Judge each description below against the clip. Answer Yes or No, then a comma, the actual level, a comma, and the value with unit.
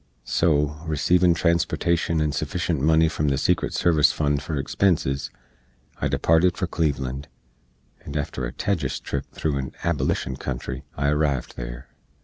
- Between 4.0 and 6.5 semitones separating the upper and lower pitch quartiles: No, average, 3.4 semitones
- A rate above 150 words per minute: No, average, 140 wpm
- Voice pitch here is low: Yes, very low, 75 Hz